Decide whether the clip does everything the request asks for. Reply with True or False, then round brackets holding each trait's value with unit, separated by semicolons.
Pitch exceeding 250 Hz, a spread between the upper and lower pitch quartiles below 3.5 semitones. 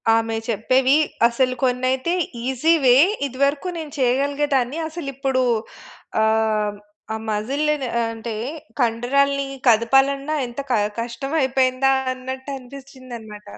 True (260 Hz; 2.8 semitones)